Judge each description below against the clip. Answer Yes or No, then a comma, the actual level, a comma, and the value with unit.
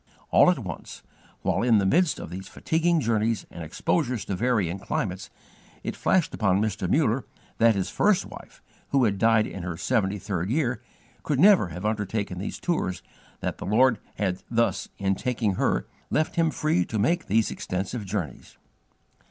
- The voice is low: Yes, low, 110 Hz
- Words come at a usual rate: Yes, average, 175 wpm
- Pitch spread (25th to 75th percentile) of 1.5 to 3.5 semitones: No, average, 4.9 semitones